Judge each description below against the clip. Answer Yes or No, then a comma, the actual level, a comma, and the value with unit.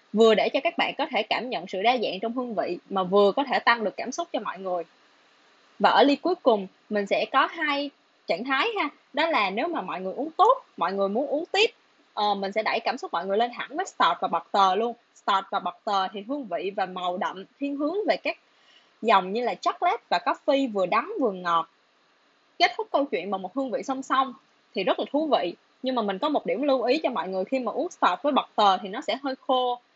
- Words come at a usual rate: No, fast, 255 wpm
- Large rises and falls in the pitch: Yes, wide, 7.0 semitones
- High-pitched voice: Yes, very high, 255 Hz